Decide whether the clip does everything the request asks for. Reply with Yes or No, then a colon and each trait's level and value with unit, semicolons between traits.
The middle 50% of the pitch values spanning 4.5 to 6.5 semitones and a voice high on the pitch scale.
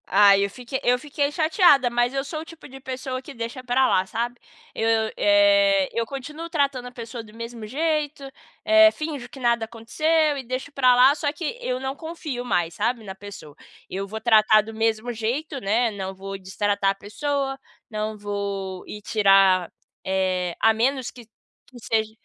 Yes: average, 4.9 semitones; high, 240 Hz